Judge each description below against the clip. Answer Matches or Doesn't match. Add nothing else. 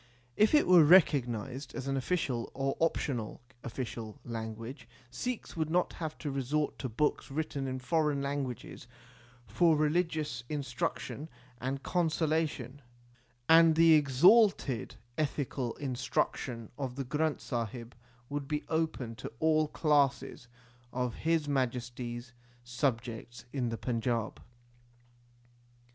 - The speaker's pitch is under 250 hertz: Matches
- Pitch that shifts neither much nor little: Matches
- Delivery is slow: Matches